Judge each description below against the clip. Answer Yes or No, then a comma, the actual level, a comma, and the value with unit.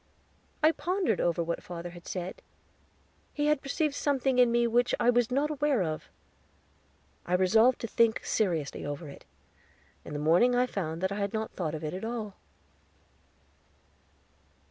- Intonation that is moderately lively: No, wide, 6.3 semitones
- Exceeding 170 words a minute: No, average, 160 wpm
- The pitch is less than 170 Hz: No, high, 220 Hz